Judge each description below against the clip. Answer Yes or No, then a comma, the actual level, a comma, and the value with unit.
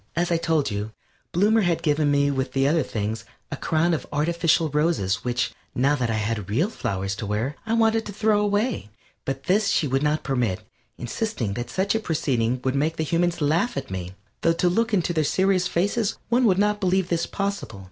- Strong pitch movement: Yes, wide, 7.3 semitones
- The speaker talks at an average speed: No, fast, 210 wpm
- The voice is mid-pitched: Yes, medium, 155 Hz